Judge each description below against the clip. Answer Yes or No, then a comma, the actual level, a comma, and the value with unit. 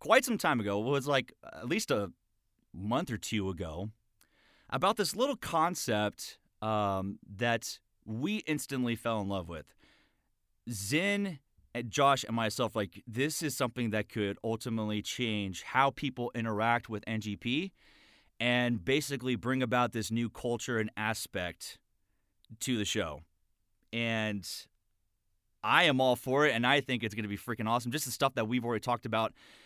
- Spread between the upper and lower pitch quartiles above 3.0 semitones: Yes, average, 3.6 semitones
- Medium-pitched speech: No, low, 115 Hz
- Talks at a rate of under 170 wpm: Yes, average, 160 wpm